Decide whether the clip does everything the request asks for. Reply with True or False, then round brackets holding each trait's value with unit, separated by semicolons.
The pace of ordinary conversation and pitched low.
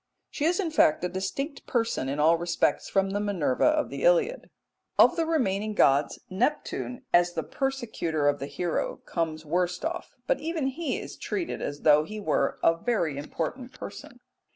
False (175 wpm; 195 Hz)